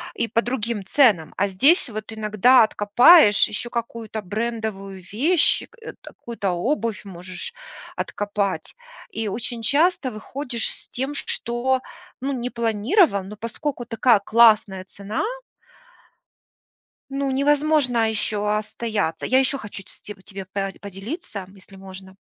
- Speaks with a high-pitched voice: Yes, high, 220 Hz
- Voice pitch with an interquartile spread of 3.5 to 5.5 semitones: Yes, average, 4.0 semitones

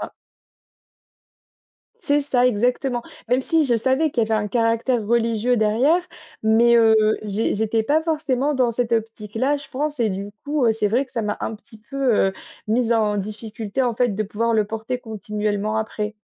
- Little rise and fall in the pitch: No, average, 3.1 semitones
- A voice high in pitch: Yes, high, 230 Hz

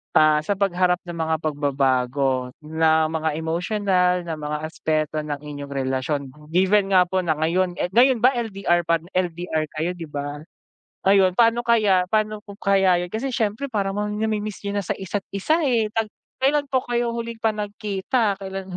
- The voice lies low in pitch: No, medium, 185 Hz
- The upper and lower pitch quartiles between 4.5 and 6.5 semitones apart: Yes, average, 5.1 semitones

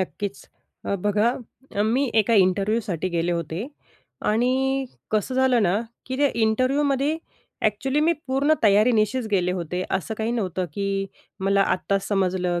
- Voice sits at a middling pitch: No, high, 210 Hz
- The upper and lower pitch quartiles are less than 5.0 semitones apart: No, average, 5.3 semitones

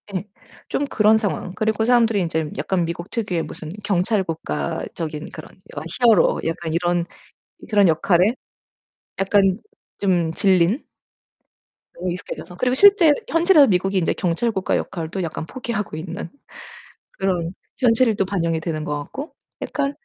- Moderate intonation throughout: Yes, average, 4.8 semitones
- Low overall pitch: No, medium, 185 Hz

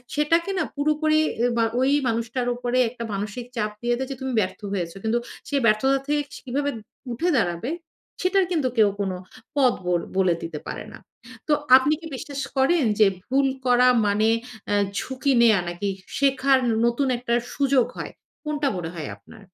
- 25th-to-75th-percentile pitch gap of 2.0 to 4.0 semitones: No, average, 4.7 semitones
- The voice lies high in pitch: Yes, very high, 250 Hz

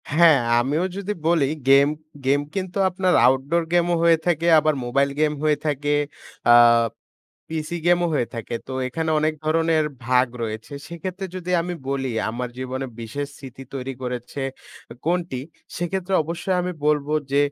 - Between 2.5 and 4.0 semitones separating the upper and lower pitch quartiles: No, average, 4.4 semitones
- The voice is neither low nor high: Yes, medium, 150 Hz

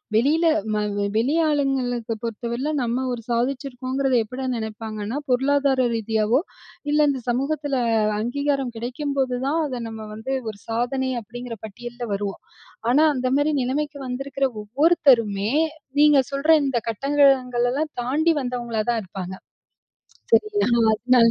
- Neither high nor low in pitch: No, very high, 250 Hz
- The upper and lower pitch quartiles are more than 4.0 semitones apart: No, average, 3.1 semitones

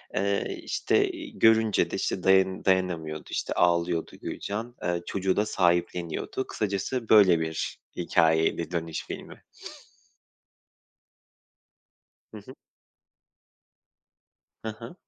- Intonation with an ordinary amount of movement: Yes, average, 3.7 semitones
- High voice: No, very low, 95 Hz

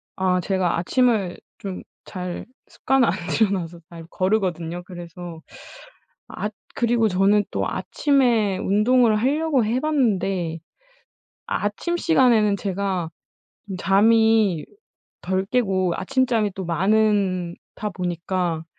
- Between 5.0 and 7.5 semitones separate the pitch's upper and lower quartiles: No, average, 3.8 semitones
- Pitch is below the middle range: No, high, 200 Hz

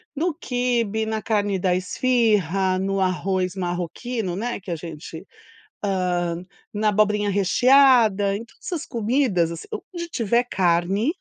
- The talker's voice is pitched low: No, high, 205 Hz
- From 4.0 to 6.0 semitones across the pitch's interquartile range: Yes, average, 4.5 semitones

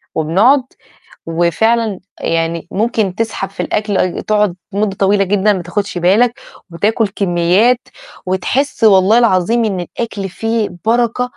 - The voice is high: Yes, high, 205 Hz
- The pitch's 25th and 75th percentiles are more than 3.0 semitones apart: Yes, average, 3.8 semitones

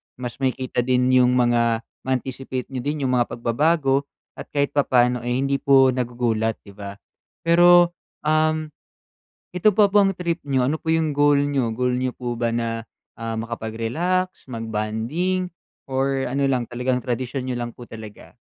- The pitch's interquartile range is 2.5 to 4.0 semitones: Yes, average, 3.4 semitones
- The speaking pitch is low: Yes, low, 130 Hz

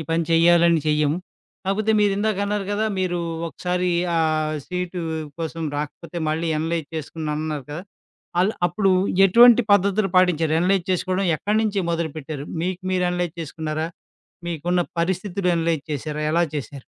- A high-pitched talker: No, medium, 170 Hz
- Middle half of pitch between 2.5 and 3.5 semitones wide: Yes, average, 3.0 semitones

